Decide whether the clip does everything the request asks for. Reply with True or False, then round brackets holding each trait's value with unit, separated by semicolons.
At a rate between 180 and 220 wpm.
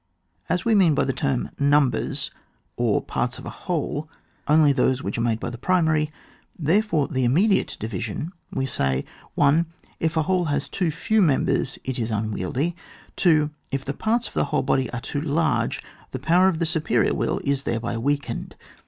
True (185 wpm)